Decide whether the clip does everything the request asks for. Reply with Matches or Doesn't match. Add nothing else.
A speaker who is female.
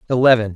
Doesn't match